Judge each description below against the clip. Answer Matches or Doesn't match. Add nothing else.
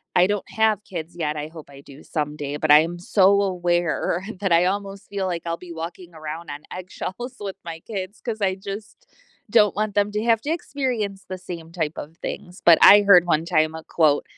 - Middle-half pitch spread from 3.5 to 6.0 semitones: Matches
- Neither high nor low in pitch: Matches